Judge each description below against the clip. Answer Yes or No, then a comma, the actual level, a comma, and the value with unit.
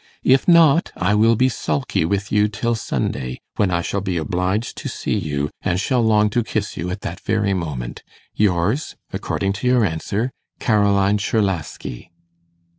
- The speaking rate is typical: Yes, average, 160 wpm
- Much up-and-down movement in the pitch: No, average, 4.0 semitones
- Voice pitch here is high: No, low, 100 Hz